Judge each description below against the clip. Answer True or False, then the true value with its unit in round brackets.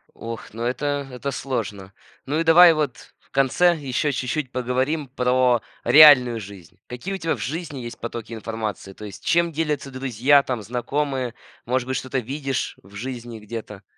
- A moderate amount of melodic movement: True (3.7 semitones)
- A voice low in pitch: True (130 Hz)